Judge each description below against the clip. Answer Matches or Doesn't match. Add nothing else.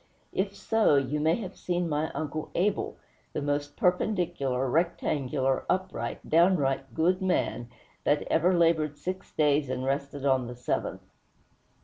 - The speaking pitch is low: Doesn't match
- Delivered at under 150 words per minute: Matches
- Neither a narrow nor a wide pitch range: Matches